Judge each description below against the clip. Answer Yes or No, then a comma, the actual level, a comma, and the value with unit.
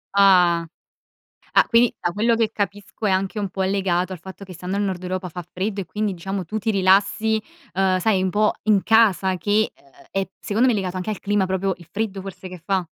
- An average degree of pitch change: No, narrow, 2.0 semitones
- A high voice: Yes, high, 195 Hz